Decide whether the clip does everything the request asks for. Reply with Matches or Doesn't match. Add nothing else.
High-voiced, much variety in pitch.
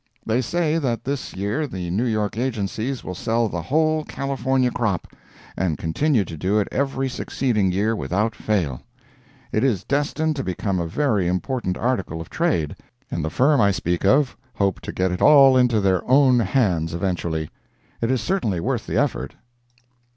Doesn't match